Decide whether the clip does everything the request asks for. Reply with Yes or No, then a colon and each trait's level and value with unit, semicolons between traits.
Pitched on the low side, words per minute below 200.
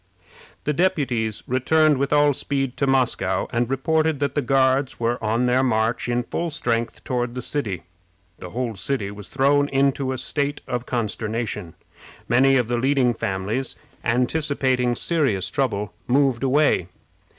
Yes: low, 130 Hz; average, 150 wpm